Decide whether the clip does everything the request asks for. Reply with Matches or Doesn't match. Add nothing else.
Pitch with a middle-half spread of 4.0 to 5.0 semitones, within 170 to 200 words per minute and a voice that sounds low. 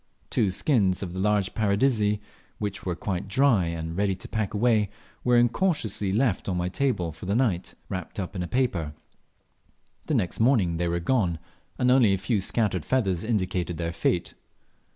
Matches